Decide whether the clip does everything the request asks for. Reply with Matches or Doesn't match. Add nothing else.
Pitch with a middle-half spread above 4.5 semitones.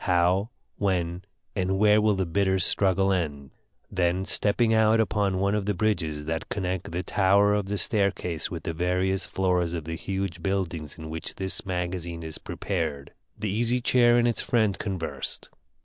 Doesn't match